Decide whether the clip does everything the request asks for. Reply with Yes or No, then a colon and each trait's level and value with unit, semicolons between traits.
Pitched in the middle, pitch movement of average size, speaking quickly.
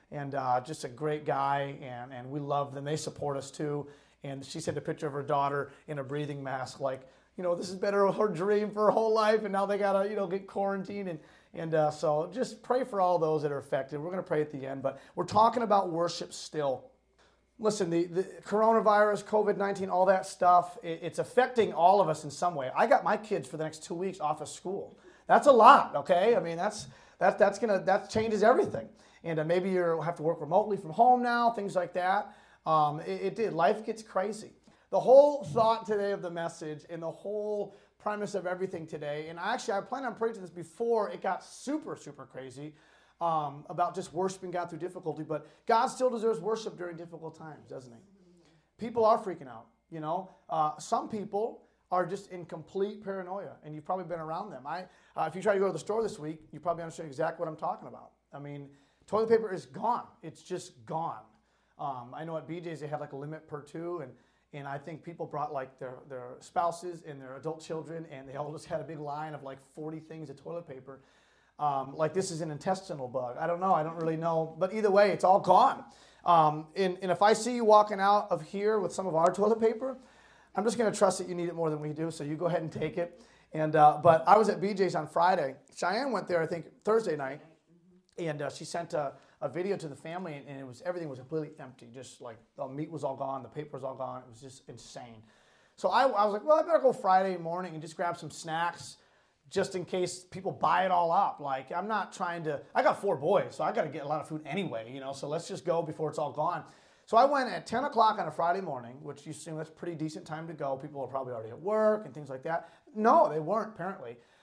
Yes: medium, 170 Hz; average, 4.6 semitones; fast, 240 wpm